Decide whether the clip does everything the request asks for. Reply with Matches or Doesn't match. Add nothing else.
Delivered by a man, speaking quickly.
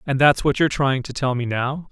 Matches